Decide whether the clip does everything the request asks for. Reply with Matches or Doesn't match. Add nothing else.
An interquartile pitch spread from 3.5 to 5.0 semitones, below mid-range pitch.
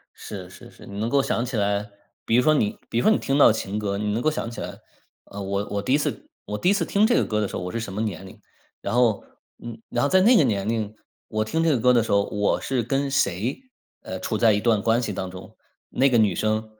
Matches